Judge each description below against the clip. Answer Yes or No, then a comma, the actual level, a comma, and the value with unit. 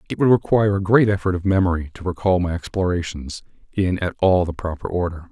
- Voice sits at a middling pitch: No, very low, 90 Hz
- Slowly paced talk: No, fast, 205 wpm